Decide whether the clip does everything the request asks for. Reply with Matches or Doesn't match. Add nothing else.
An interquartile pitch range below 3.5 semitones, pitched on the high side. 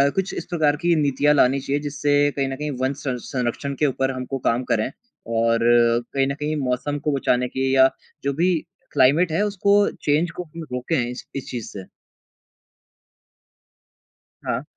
Doesn't match